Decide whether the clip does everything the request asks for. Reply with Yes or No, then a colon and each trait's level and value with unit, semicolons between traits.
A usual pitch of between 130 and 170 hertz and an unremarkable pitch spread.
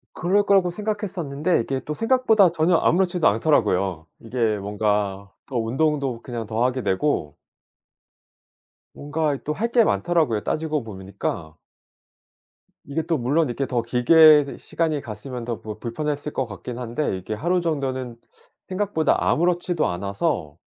No: medium, 140 Hz; wide, 6.6 semitones